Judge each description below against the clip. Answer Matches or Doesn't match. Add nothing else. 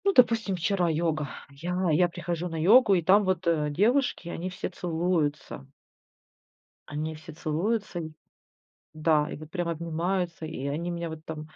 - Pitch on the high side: Doesn't match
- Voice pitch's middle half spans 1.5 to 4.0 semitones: Matches